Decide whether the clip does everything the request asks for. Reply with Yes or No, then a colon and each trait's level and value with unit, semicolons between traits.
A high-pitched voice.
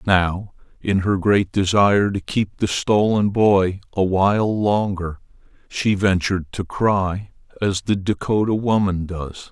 No: low, 100 Hz